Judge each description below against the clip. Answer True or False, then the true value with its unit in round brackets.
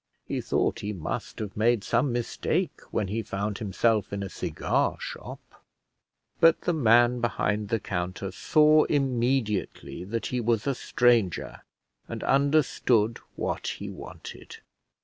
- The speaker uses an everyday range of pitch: True (3.4 semitones)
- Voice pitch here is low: True (115 Hz)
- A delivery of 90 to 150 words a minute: True (135 wpm)